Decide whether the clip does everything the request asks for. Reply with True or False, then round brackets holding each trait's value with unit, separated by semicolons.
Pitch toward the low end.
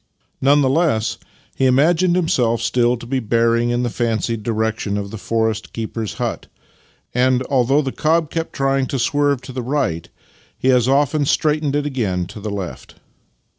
True (125 Hz)